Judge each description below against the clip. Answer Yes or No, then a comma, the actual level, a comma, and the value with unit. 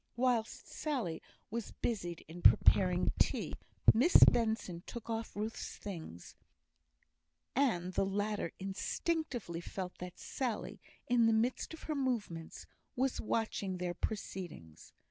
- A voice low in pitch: No, high, 210 Hz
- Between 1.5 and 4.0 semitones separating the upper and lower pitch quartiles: No, average, 5.0 semitones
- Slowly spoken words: Yes, slow, 120 wpm